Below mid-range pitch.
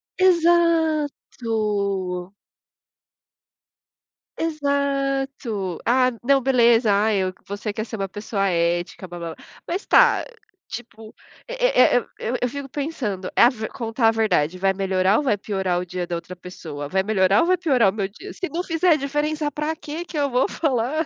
No: high, 230 Hz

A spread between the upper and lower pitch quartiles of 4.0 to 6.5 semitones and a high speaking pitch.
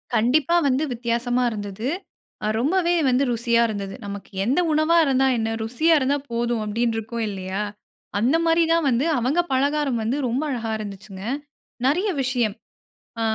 Yes: average, 4.3 semitones; high, 240 Hz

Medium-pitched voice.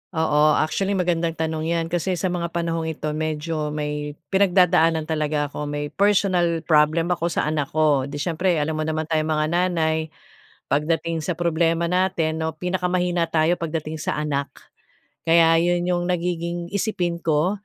Yes: medium, 165 Hz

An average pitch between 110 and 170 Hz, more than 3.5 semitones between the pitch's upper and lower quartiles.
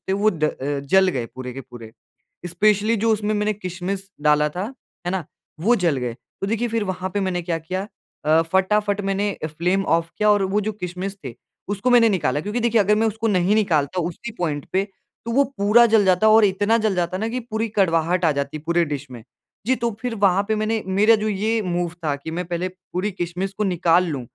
No: high, 190 Hz; average, 4.0 semitones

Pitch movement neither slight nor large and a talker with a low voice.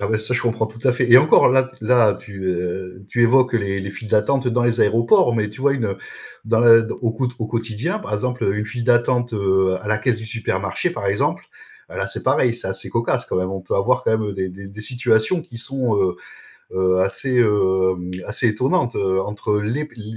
Yes: average, 3.6 semitones; low, 110 Hz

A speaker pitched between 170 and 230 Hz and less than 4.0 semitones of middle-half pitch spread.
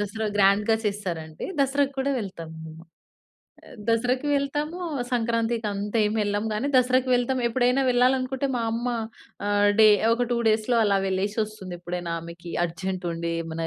No: high, 215 Hz; average, 4.8 semitones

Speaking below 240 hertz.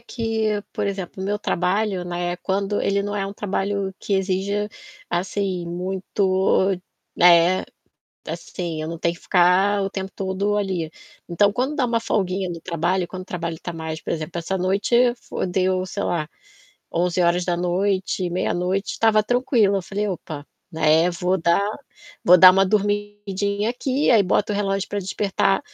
Yes: high, 190 Hz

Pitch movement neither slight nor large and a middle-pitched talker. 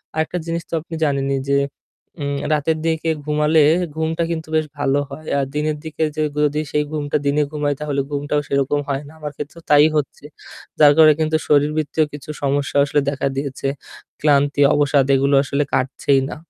No: narrow, 1.6 semitones; medium, 145 Hz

